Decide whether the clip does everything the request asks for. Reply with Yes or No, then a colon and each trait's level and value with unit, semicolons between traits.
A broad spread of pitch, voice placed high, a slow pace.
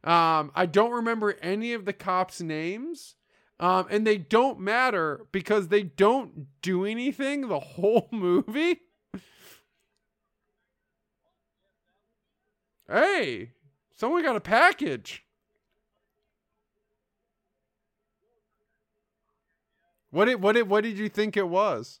No: average, 4.1 semitones; high, 215 Hz; slow, 100 wpm